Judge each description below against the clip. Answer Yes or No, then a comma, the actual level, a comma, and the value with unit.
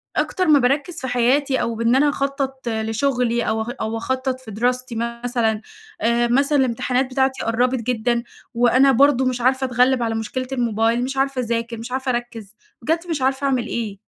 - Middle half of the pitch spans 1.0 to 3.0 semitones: Yes, narrow, 2.4 semitones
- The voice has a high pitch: Yes, very high, 250 Hz